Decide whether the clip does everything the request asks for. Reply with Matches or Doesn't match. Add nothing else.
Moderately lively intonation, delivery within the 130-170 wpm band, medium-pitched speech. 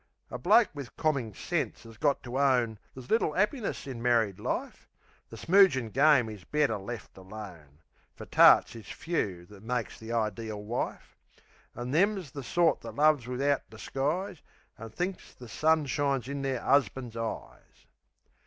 Doesn't match